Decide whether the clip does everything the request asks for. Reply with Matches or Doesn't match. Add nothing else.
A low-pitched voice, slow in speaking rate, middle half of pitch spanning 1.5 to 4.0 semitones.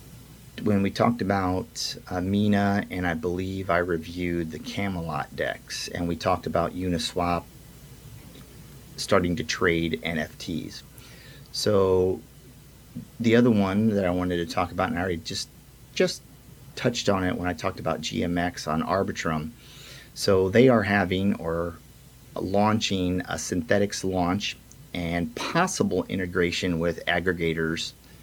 Doesn't match